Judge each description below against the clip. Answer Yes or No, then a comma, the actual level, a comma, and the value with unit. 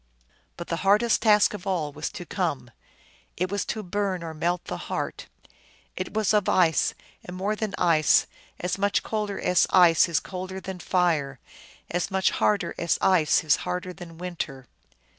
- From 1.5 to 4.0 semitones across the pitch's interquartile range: Yes, average, 2.8 semitones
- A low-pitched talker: No, medium, 180 Hz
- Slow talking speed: No, average, 170 wpm